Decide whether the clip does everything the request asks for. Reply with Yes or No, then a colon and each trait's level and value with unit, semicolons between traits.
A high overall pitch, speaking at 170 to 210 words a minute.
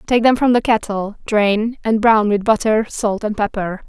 Yes: high, 215 Hz; average, 200 wpm